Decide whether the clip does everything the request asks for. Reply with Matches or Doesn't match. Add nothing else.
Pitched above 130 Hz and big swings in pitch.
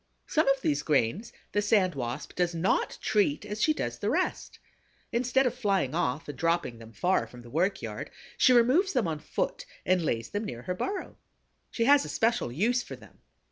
Matches